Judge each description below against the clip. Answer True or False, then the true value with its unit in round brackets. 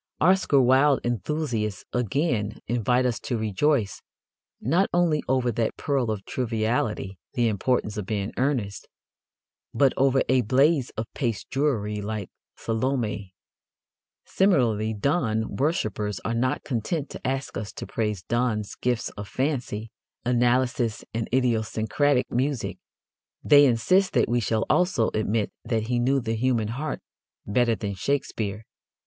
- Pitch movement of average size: True (3.7 semitones)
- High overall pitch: False (120 Hz)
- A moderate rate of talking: False (130 wpm)